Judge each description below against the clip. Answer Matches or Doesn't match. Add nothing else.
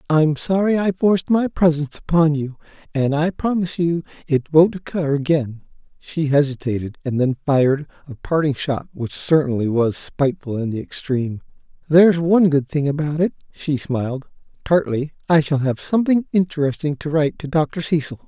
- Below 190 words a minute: Matches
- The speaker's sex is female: Doesn't match